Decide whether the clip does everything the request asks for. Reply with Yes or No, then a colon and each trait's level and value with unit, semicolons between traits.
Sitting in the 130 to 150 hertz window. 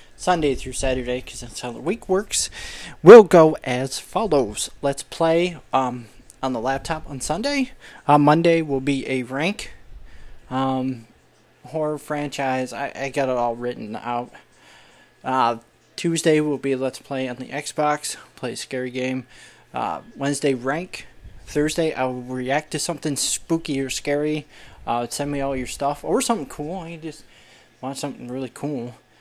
Yes: medium, 140 Hz